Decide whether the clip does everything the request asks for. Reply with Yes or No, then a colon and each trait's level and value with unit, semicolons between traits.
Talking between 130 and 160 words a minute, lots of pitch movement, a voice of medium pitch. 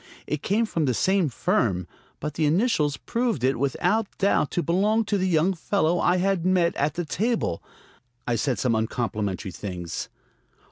No: average, 170 wpm; wide, 7.3 semitones; medium, 165 Hz